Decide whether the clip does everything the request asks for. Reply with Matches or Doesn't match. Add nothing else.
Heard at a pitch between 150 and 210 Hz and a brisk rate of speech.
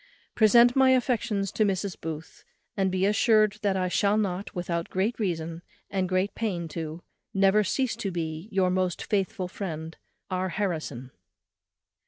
Doesn't match